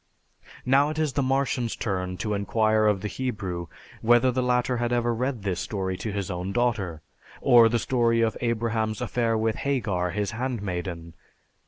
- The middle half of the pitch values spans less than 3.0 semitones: No, average, 3.7 semitones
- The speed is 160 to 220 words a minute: Yes, average, 170 wpm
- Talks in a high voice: No, low, 115 Hz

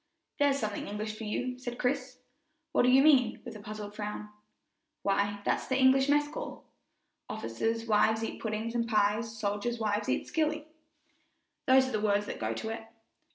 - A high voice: Yes, high, 225 Hz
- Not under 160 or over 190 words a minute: Yes, average, 170 wpm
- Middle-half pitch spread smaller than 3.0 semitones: No, average, 3.7 semitones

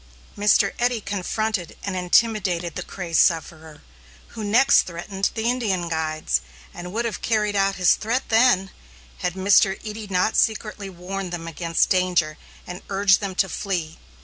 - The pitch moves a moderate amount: Yes, average, 3.3 semitones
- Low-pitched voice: No, high, 195 Hz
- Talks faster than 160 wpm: No, average, 150 wpm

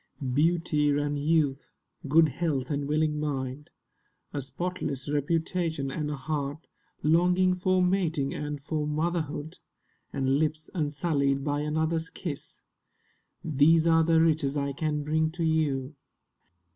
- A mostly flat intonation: Yes, narrow, 2.2 semitones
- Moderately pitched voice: Yes, medium, 150 Hz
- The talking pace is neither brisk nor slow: No, slow, 125 wpm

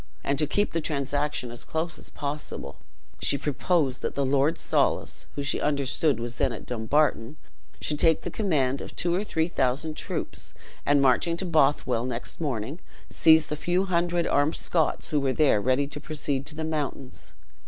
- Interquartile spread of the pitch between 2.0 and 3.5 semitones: Yes, average, 3.1 semitones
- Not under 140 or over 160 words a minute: No, average, 180 wpm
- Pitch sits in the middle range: Yes, medium, 145 Hz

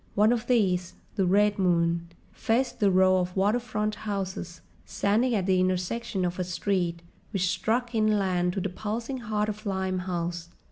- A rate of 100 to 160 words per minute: Yes, average, 155 wpm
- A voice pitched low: No, high, 195 Hz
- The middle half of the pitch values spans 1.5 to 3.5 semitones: Yes, average, 2.9 semitones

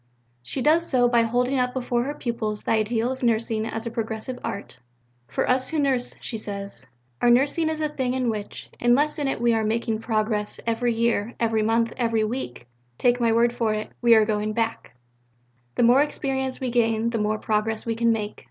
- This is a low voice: No, high, 235 Hz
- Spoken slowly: No, fast, 205 wpm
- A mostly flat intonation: Yes, narrow, 2.3 semitones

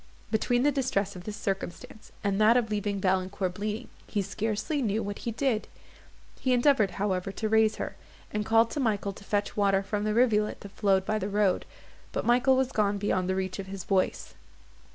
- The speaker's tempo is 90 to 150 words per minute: No, average, 195 wpm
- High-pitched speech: Yes, high, 210 Hz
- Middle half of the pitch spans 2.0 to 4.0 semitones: Yes, narrow, 2.4 semitones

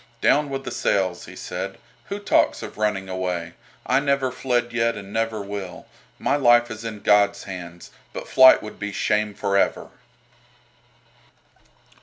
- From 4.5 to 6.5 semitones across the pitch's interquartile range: No, average, 3.7 semitones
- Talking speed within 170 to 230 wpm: No, average, 155 wpm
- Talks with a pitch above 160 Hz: No, low, 105 Hz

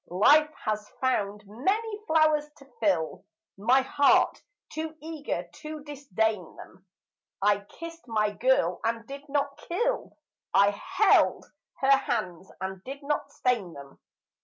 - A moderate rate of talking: No, slow, 130 wpm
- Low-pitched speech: No, very high, 260 Hz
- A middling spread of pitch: No, wide, 6.9 semitones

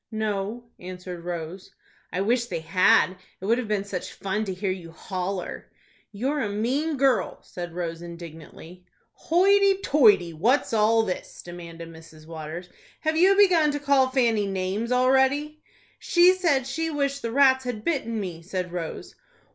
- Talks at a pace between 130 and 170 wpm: Yes, average, 155 wpm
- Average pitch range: No, wide, 7.1 semitones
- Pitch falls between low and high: No, high, 210 Hz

